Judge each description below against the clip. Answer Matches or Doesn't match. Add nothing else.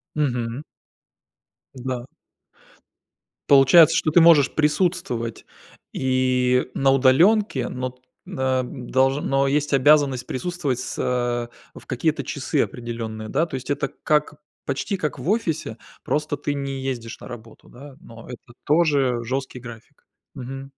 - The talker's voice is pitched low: Matches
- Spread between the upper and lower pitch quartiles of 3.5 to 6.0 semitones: Doesn't match